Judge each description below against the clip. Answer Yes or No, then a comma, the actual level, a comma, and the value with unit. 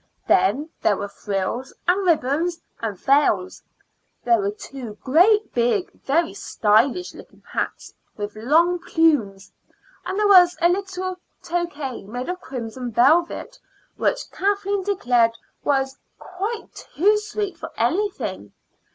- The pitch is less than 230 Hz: No, very high, 305 Hz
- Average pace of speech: No, slow, 125 wpm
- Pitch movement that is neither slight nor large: No, wide, 7.7 semitones